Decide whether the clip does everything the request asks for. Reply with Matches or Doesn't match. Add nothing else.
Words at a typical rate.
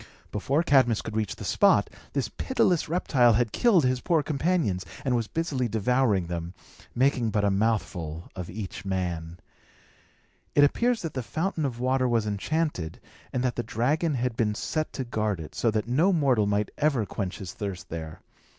Matches